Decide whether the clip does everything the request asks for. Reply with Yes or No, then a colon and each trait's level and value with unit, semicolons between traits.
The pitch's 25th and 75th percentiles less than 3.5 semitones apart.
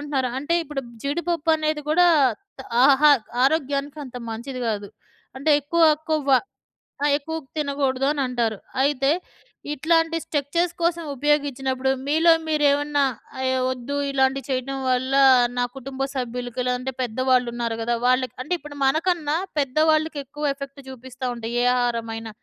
Yes: average, 2.8 semitones